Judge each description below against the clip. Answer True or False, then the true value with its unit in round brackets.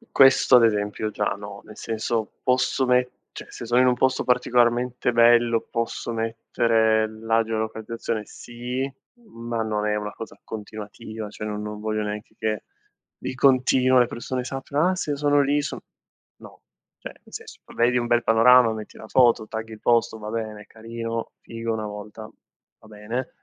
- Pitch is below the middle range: True (115 Hz)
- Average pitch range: False (2.3 semitones)